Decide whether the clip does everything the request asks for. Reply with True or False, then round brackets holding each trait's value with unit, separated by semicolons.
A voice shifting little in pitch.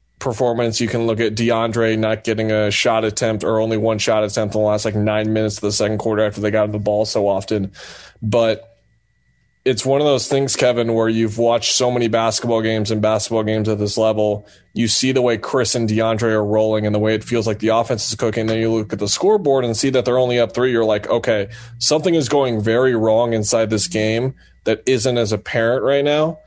True (1.7 semitones)